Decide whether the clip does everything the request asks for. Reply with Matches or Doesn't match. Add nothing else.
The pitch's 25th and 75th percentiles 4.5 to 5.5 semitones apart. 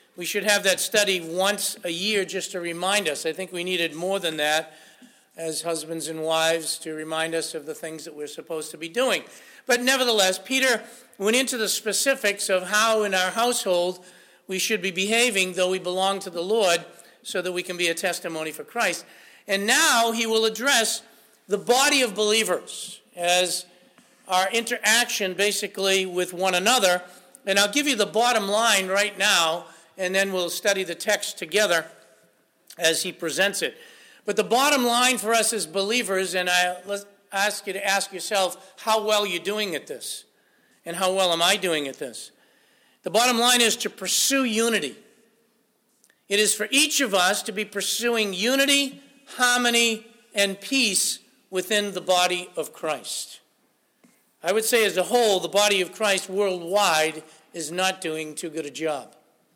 Doesn't match